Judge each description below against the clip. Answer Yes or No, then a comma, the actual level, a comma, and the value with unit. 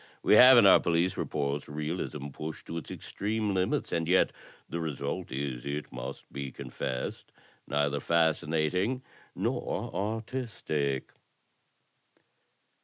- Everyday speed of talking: No, slow, 115 wpm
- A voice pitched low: Yes, very low, 80 Hz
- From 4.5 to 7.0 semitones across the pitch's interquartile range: Yes, average, 5.0 semitones